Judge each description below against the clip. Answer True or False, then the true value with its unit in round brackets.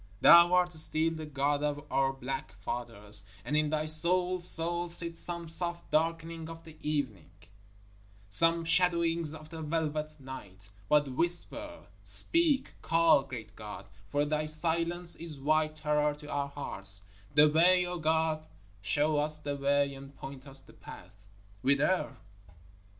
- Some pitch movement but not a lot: True (3.2 semitones)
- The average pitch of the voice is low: False (155 Hz)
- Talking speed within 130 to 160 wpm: True (145 wpm)